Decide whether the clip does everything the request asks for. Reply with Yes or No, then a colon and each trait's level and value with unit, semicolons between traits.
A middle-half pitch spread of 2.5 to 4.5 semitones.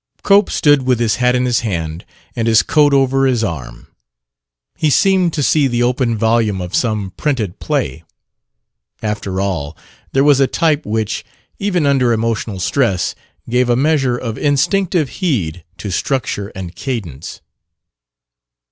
No: wide, 5.5 semitones